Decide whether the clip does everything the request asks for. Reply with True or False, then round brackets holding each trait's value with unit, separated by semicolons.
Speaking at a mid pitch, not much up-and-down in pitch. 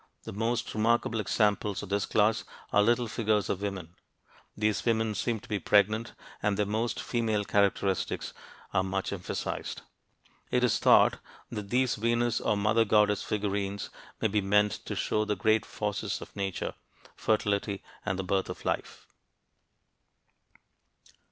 False (105 Hz; 1.8 semitones)